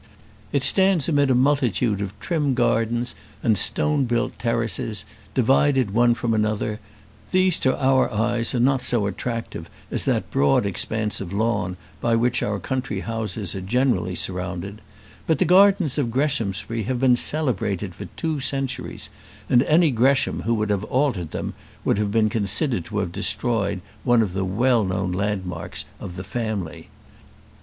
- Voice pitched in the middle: No, low, 115 Hz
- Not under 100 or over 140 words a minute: No, average, 160 wpm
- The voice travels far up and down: No, average, 4.6 semitones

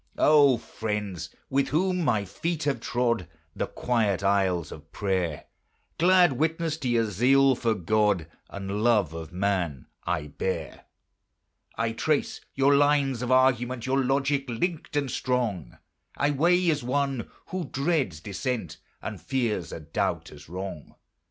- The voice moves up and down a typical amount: No, wide, 6.3 semitones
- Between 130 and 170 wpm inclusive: Yes, average, 140 wpm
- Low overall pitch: Yes, low, 120 Hz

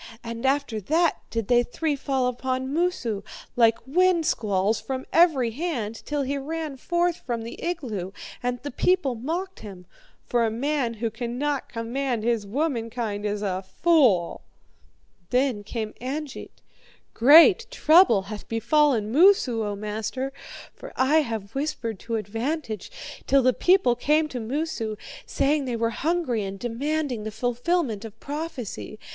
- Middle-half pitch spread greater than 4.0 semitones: Yes, average, 5.1 semitones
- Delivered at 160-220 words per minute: No, average, 145 wpm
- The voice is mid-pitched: No, very high, 250 Hz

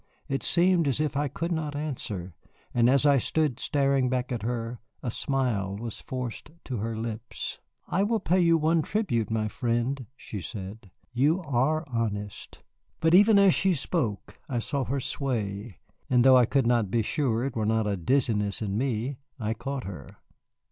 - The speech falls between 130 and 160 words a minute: No, average, 180 wpm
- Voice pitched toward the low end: Yes, low, 125 Hz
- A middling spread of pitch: Yes, average, 4.5 semitones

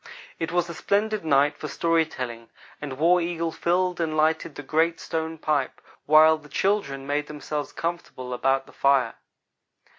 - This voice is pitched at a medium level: Yes, medium, 155 Hz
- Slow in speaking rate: No, average, 160 wpm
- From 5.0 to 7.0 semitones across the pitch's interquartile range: No, average, 3.2 semitones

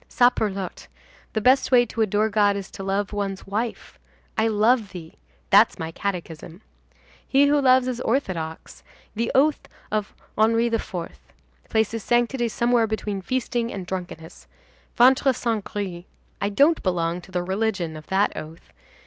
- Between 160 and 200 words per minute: No, average, 150 wpm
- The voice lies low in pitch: No, high, 210 Hz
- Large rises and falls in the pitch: No, average, 4.1 semitones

